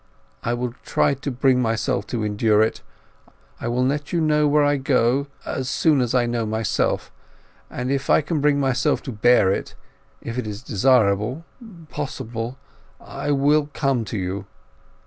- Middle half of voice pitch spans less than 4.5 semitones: Yes, average, 3.7 semitones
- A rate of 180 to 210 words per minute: No, average, 165 wpm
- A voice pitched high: No, low, 125 Hz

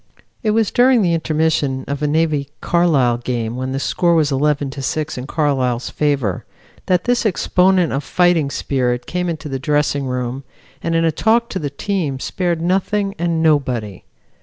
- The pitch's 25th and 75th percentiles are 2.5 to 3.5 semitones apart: No, average, 4.7 semitones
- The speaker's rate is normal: Yes, average, 175 wpm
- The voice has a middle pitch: Yes, medium, 150 Hz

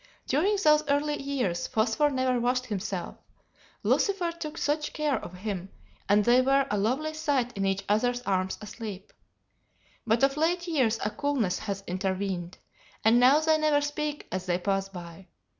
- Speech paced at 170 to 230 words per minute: No, average, 160 wpm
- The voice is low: No, high, 245 Hz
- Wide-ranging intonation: Yes, wide, 7.0 semitones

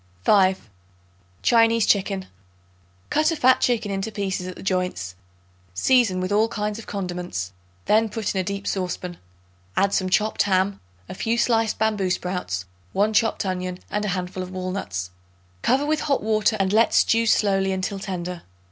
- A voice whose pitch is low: No, high, 195 Hz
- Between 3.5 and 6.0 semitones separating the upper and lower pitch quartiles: No, average, 3.1 semitones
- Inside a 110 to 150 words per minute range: No, average, 165 wpm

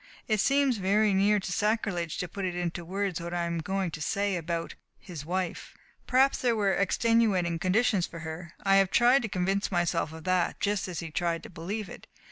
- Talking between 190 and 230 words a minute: Yes, average, 200 wpm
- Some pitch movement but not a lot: Yes, average, 3.4 semitones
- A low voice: No, medium, 185 Hz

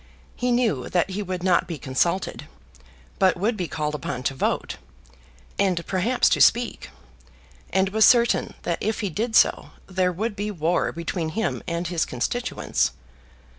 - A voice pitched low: No, medium, 185 Hz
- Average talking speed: Yes, average, 160 wpm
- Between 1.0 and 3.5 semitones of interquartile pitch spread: No, average, 4.1 semitones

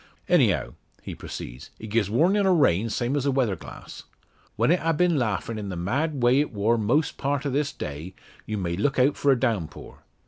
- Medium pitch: No, low, 120 Hz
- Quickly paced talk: Yes, fast, 210 wpm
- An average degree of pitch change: No, wide, 6.1 semitones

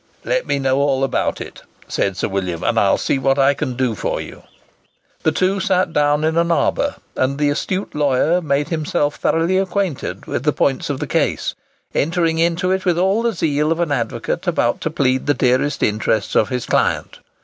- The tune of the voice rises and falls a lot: No, average, 4.4 semitones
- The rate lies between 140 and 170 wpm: No, average, 200 wpm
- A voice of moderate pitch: Yes, medium, 150 Hz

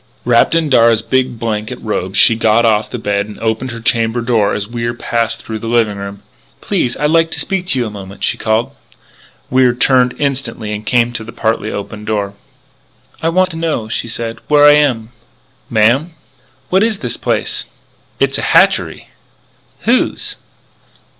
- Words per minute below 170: No, average, 180 wpm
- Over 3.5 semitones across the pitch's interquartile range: No, average, 3.2 semitones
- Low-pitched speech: Yes, low, 115 Hz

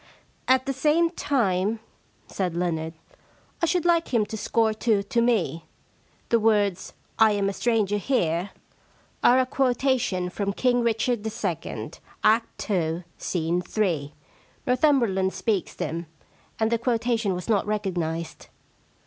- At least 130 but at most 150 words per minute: Yes, average, 140 wpm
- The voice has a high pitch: Yes, high, 215 Hz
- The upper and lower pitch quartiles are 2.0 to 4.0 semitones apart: No, average, 5.0 semitones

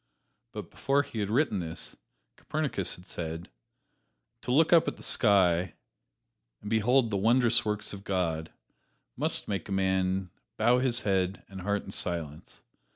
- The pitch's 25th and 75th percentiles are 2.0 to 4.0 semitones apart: No, average, 4.5 semitones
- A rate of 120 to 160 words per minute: Yes, average, 155 wpm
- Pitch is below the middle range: Yes, low, 100 Hz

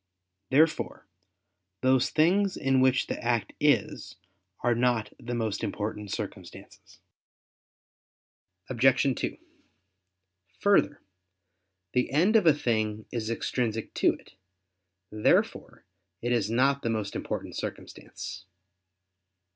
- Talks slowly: Yes, slow, 105 wpm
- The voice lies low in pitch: Yes, low, 120 Hz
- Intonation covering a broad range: No, average, 3.9 semitones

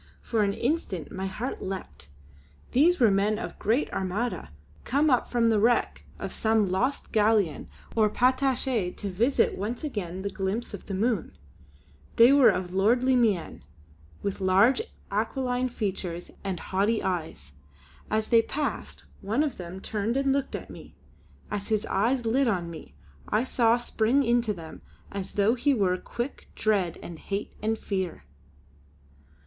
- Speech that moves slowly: No, average, 155 wpm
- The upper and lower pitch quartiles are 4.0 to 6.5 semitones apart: Yes, average, 4.3 semitones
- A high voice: Yes, high, 215 Hz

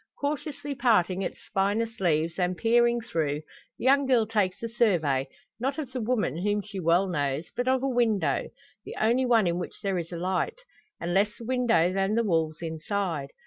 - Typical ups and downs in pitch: No, wide, 5.8 semitones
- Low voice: No, high, 200 Hz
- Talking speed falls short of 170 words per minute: No, average, 190 wpm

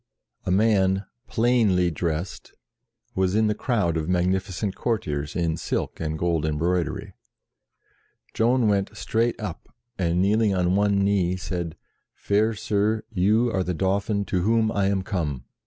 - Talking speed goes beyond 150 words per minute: No, average, 140 wpm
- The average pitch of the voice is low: Yes, very low, 95 Hz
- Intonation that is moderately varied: Yes, average, 3.4 semitones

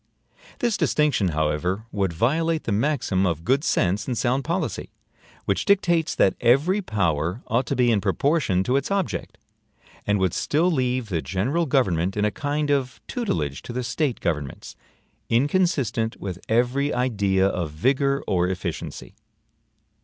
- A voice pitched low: Yes, low, 120 Hz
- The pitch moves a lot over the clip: Yes, wide, 7.2 semitones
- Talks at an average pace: Yes, average, 150 wpm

